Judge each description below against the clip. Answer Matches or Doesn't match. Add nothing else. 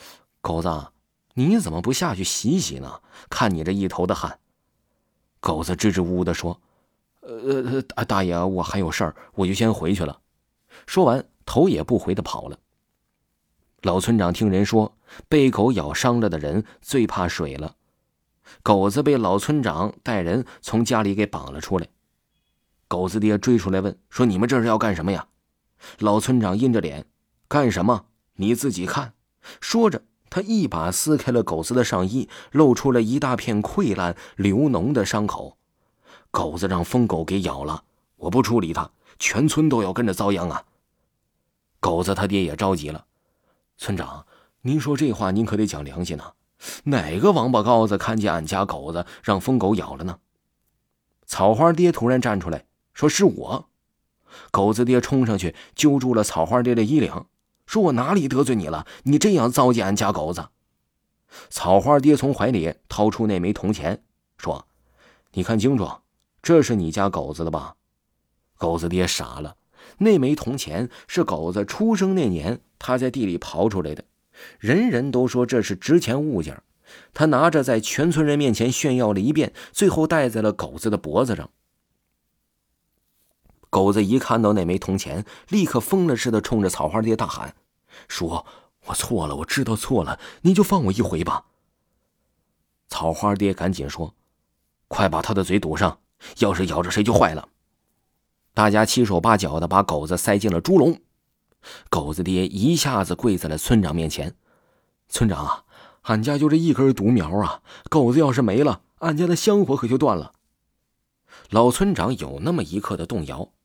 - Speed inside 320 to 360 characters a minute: Doesn't match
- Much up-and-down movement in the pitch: Matches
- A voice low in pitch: Matches